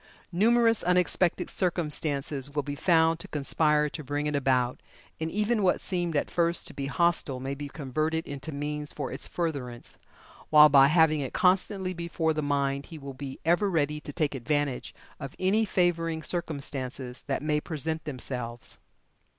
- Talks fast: No, average, 165 wpm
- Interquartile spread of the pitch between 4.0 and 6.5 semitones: No, average, 3.4 semitones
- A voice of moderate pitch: Yes, medium, 150 Hz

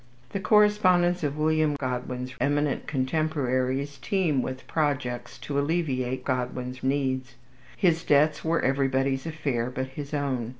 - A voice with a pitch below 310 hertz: Yes, medium, 140 Hz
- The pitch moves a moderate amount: Yes, average, 3.3 semitones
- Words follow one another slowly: Yes, slow, 125 wpm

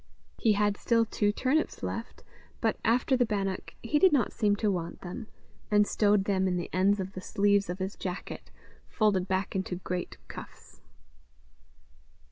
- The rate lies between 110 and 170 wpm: Yes, average, 165 wpm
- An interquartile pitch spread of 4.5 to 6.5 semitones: No, narrow, 2.5 semitones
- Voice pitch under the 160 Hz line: No, high, 205 Hz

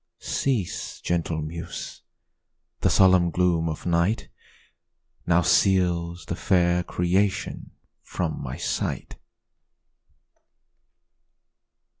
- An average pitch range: No, narrow, 1.6 semitones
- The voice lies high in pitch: No, very low, 85 Hz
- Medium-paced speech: No, slow, 80 wpm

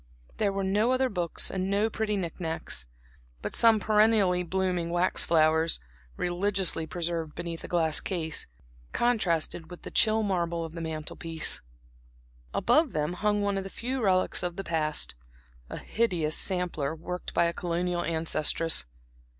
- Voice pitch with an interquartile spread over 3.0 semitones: Yes, average, 3.6 semitones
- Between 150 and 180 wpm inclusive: Yes, average, 155 wpm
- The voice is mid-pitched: Yes, medium, 180 Hz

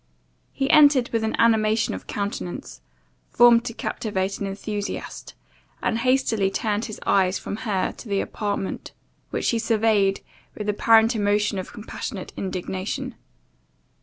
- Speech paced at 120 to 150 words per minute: Yes, slow, 135 wpm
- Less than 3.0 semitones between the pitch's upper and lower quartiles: Yes, narrow, 2.5 semitones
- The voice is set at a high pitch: Yes, high, 210 Hz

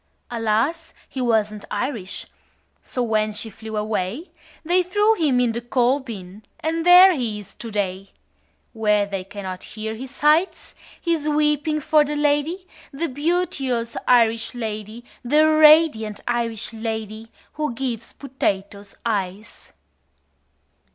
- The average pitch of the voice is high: Yes, high, 235 Hz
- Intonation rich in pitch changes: Yes, wide, 5.8 semitones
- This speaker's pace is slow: Yes, slow, 130 wpm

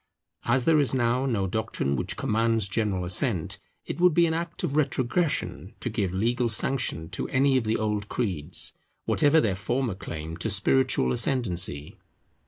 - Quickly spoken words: No, average, 165 wpm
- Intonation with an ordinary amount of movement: No, wide, 6.1 semitones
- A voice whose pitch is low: Yes, low, 115 Hz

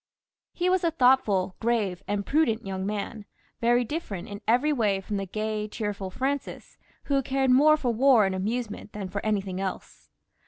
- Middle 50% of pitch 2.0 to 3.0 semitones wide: No, average, 4.9 semitones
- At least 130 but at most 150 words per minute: No, average, 170 wpm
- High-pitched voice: Yes, high, 215 Hz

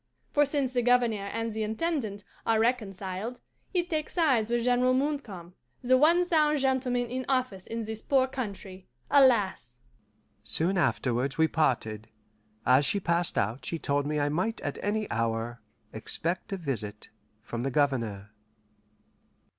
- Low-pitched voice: No, high, 210 Hz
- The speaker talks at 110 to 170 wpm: Yes, average, 145 wpm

